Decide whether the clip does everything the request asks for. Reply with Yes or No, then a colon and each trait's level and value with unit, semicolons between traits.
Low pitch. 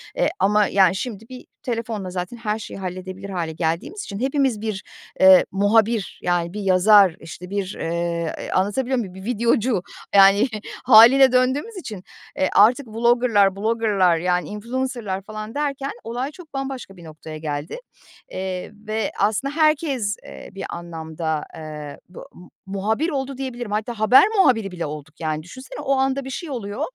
No: high, 210 Hz